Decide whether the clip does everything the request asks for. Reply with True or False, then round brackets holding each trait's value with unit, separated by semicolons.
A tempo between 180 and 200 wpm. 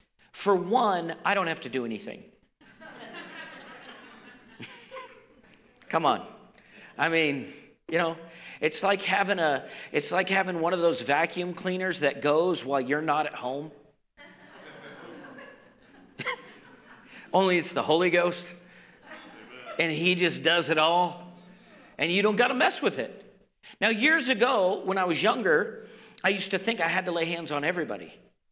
False (145 wpm)